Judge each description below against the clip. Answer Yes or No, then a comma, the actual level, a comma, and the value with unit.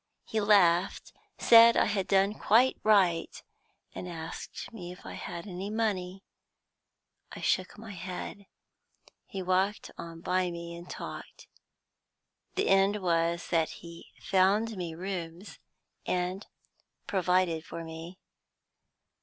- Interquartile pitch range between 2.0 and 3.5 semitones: Yes, average, 2.8 semitones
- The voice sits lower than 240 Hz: Yes, medium, 185 Hz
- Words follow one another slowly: Yes, slow, 120 wpm